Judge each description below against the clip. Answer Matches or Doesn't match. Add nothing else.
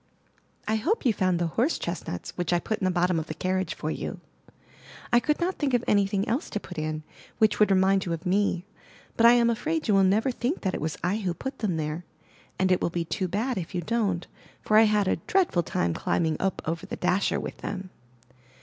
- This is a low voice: Doesn't match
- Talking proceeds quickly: Matches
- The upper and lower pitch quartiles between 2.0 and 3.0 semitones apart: Doesn't match